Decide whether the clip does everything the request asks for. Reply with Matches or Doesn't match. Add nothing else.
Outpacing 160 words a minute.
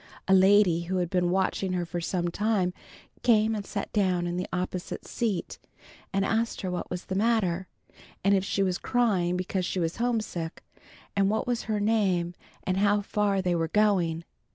Matches